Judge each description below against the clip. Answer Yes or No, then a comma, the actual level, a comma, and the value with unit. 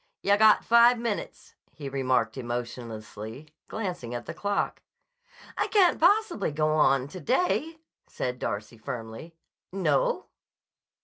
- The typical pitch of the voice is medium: Yes, medium, 155 Hz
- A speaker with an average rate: No, slow, 120 wpm